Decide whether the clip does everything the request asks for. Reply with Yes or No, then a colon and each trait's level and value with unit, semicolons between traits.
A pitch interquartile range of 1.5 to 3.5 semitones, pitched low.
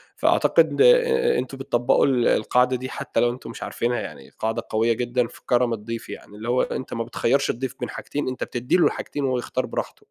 Yes: narrow, 2.5 semitones; low, 125 Hz